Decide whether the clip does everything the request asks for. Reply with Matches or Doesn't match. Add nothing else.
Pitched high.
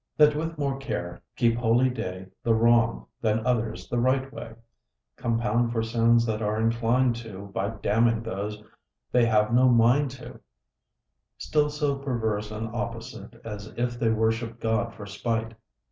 Doesn't match